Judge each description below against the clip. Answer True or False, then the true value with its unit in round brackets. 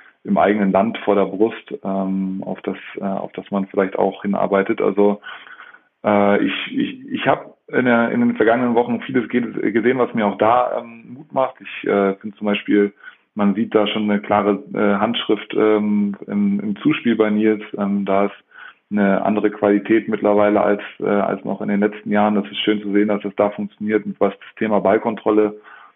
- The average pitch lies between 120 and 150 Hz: False (105 Hz)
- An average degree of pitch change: False (1.7 semitones)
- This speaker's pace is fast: True (195 wpm)